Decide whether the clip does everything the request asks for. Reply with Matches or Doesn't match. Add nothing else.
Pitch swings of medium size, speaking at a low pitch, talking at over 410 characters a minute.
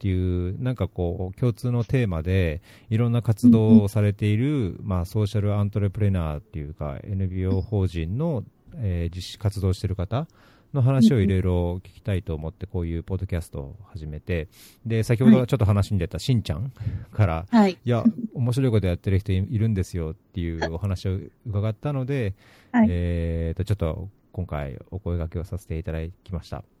Doesn't match